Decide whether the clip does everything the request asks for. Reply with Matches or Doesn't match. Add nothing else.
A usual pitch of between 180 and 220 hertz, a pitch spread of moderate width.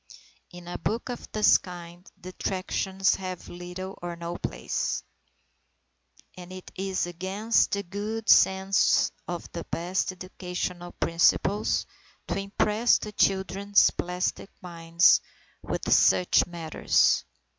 Doesn't match